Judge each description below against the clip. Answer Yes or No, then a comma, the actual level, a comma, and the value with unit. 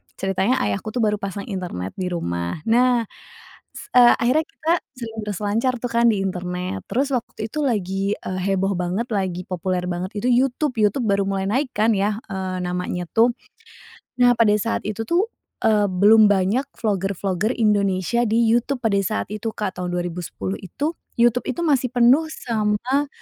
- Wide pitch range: No, average, 4.3 semitones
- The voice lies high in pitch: Yes, high, 210 Hz